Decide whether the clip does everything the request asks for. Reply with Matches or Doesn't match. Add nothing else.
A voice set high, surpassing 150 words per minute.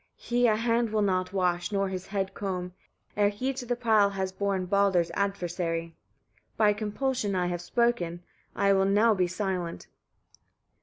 Matches